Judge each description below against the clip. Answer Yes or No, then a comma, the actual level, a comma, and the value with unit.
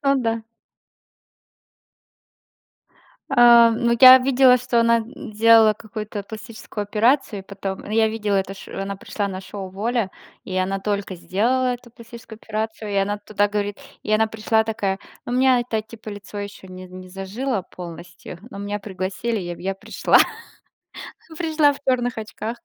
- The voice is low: No, high, 215 Hz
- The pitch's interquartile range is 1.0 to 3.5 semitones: Yes, average, 3.1 semitones